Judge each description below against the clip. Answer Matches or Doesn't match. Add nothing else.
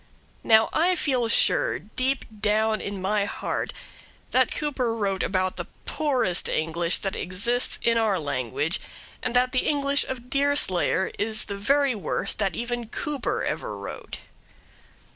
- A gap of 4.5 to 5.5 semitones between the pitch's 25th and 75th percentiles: Matches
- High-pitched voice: Matches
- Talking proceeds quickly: Doesn't match